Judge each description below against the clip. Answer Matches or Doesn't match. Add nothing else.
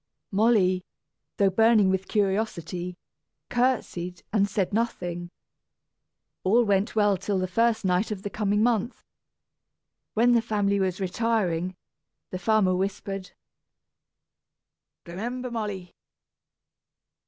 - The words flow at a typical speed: Doesn't match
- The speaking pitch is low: Doesn't match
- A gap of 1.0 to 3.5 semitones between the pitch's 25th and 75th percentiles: Matches